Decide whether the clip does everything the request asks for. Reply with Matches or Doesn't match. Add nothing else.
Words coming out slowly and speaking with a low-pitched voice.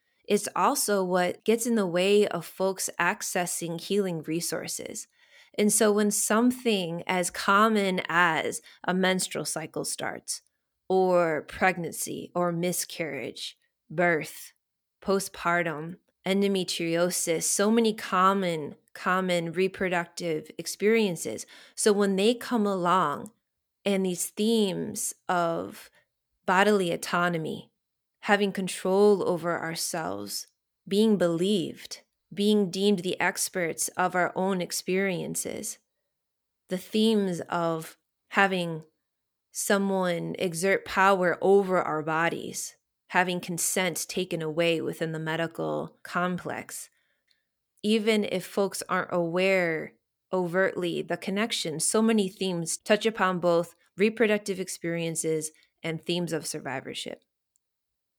Doesn't match